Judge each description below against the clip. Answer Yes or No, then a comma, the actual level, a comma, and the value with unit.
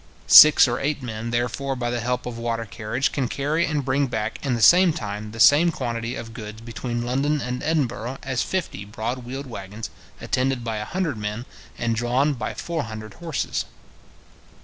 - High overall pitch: No, low, 120 Hz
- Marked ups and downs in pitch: No, average, 3.6 semitones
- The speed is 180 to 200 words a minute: Yes, average, 185 wpm